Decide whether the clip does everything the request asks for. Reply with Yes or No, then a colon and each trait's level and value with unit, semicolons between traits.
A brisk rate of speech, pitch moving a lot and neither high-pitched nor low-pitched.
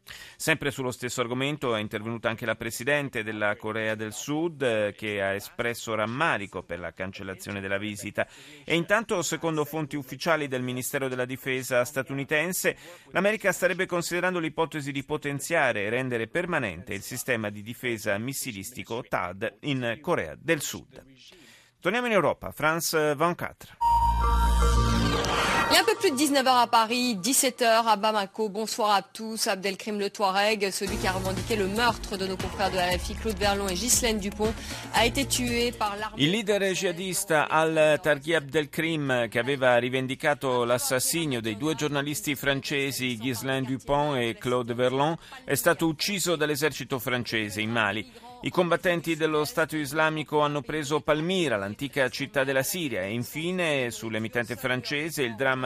No: average, 150 wpm; wide, 6.3 semitones; medium, 150 Hz